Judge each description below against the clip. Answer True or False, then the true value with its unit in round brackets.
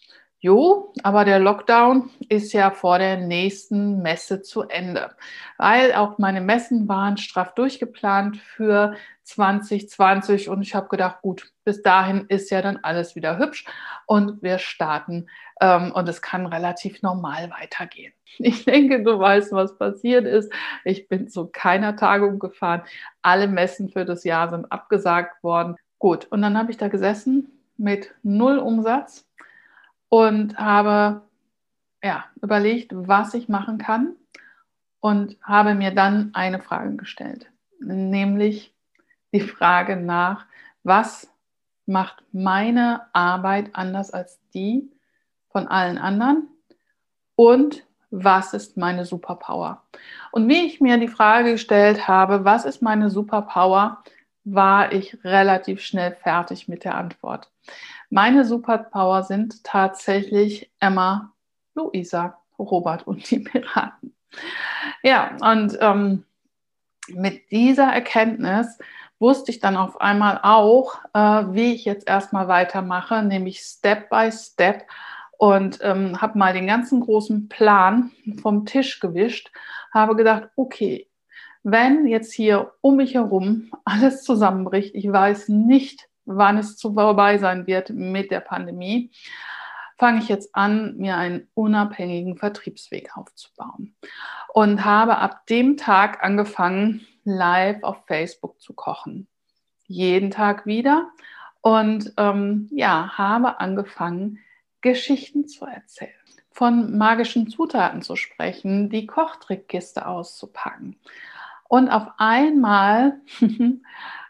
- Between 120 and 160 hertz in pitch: False (205 Hz)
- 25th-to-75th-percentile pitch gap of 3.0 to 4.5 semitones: True (3.5 semitones)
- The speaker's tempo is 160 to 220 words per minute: False (125 wpm)